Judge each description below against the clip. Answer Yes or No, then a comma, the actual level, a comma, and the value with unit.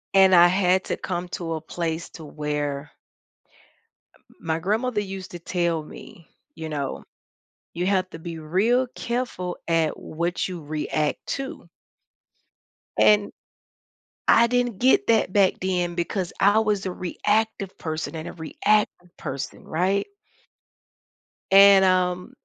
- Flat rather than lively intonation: No, average, 3.5 semitones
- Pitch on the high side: No, medium, 180 Hz